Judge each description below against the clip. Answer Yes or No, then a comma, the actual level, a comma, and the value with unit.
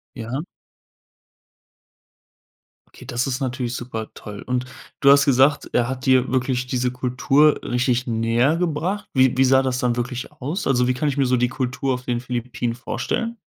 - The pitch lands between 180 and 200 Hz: No, low, 125 Hz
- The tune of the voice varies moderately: No, narrow, 1.7 semitones